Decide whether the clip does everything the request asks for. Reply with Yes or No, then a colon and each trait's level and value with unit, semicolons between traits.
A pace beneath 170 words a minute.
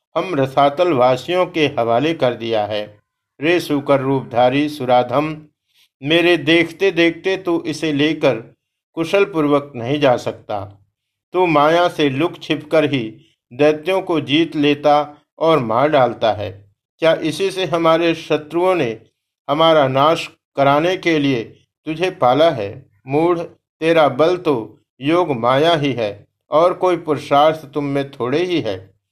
Yes: average, 135 wpm